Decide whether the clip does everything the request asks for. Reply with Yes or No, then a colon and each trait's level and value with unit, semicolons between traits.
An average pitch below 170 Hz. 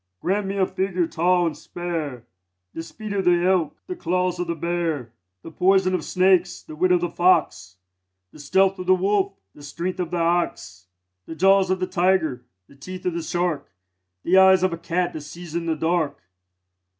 No: medium, 175 Hz